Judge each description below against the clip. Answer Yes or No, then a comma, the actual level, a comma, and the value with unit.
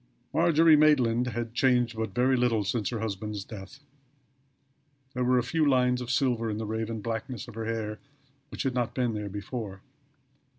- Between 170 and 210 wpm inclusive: Yes, average, 175 wpm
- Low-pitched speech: Yes, low, 115 Hz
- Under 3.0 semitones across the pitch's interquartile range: Yes, narrow, 2.5 semitones